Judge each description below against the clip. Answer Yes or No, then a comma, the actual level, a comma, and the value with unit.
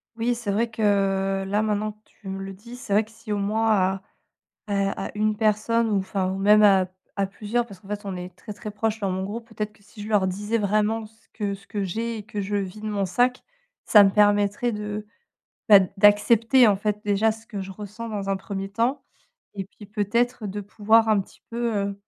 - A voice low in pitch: No, high, 210 Hz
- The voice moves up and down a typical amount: No, narrow, 2.0 semitones